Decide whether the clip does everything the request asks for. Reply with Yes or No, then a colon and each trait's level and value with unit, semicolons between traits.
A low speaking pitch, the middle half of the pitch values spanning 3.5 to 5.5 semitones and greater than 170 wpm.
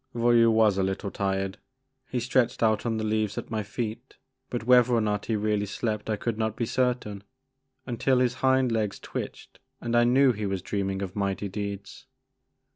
No: low, 110 Hz; average, 2.8 semitones; average, 190 wpm